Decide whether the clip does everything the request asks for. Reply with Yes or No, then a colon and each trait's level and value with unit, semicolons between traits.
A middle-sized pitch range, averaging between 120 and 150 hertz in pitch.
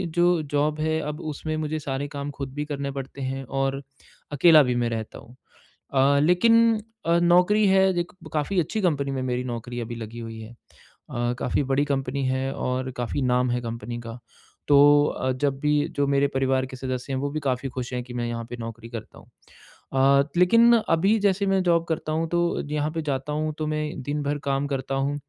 Yes: average, 3.6 semitones; medium, 140 Hz